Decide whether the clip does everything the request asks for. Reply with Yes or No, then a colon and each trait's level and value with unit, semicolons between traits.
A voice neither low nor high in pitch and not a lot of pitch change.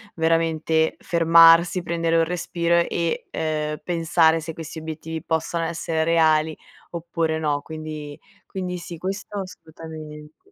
Yes: medium, 165 Hz; narrow, 1.1 semitones